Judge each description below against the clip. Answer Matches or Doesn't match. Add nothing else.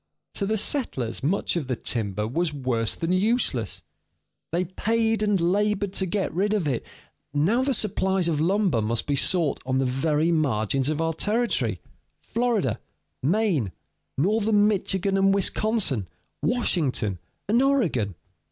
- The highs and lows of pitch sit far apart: Matches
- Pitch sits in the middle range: Matches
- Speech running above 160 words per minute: Doesn't match